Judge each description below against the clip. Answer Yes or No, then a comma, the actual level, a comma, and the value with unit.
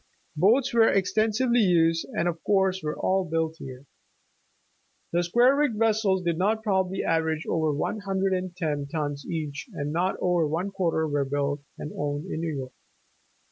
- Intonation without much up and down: No, average, 4.2 semitones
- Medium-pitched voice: Yes, medium, 175 Hz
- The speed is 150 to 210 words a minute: Yes, average, 170 wpm